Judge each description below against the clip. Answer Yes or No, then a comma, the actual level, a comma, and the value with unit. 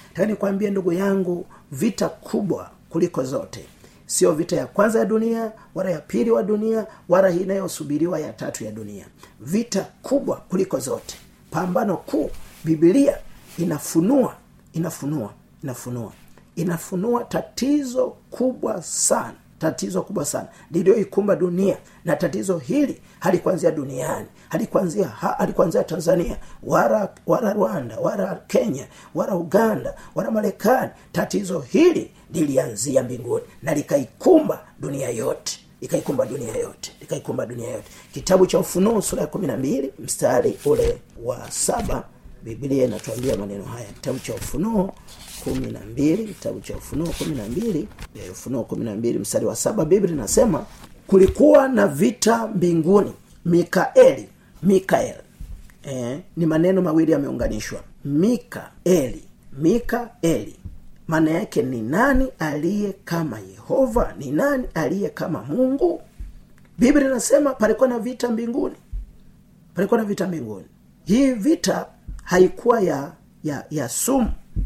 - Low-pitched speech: No, high, 190 Hz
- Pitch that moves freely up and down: Yes, wide, 6.4 semitones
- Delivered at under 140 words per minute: Yes, average, 115 wpm